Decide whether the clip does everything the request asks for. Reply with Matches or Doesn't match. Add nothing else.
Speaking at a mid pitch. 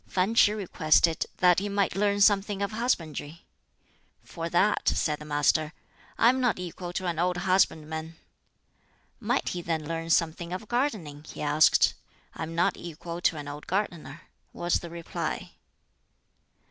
Matches